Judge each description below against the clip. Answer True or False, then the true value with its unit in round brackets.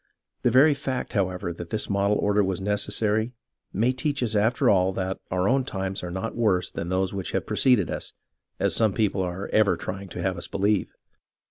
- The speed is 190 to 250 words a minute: True (205 wpm)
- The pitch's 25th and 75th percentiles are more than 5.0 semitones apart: False (2.9 semitones)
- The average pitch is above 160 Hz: False (100 Hz)